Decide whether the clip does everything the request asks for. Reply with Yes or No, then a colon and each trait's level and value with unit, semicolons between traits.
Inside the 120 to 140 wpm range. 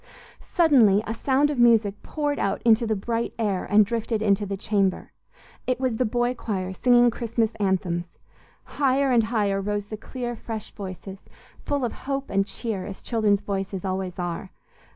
No: average, 170 wpm